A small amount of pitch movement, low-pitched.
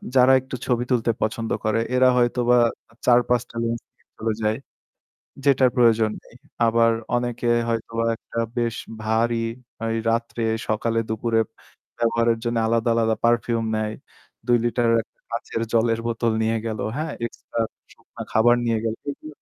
Yes: narrow, 1.1 semitones; low, 115 Hz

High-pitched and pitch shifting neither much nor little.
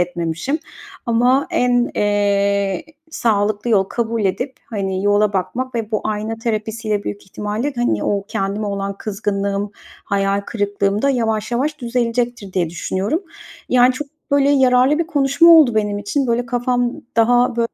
Yes: high, 220 Hz; average, 3.6 semitones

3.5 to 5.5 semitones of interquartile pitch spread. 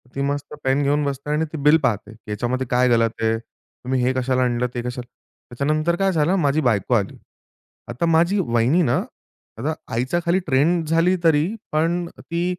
Yes: average, 4.9 semitones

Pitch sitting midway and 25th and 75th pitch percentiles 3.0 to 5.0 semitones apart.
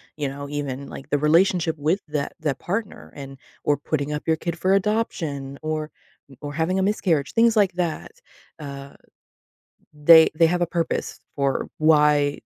Yes: medium, 155 Hz; average, 3.5 semitones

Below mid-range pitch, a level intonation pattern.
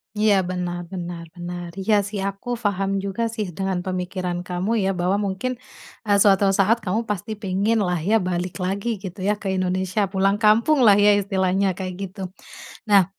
No: high, 195 Hz; narrow, 2.2 semitones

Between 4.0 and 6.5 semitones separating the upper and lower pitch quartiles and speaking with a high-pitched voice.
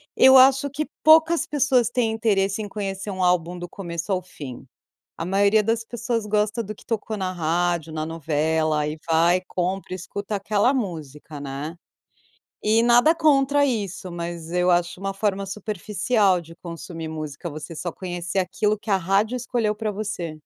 Yes: average, 4.5 semitones; high, 195 Hz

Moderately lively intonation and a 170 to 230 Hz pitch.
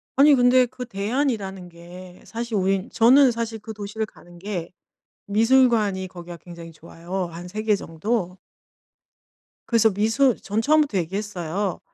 Yes: average, 4.4 semitones; high, 205 Hz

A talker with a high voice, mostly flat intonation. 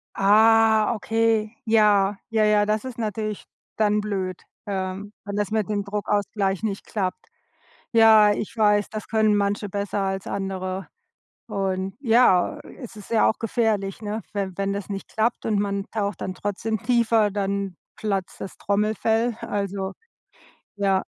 Yes: high, 205 Hz; narrow, 1.8 semitones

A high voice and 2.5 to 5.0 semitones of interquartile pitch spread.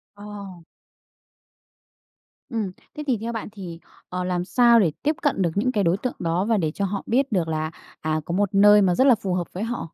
Yes: high, 200 Hz; average, 4.3 semitones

